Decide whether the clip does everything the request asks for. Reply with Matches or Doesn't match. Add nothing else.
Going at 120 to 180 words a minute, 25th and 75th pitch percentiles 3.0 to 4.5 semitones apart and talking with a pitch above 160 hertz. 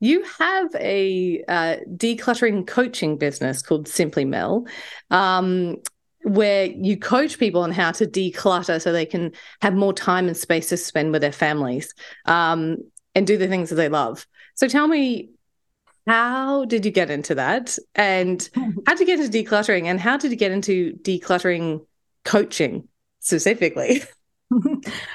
Doesn't match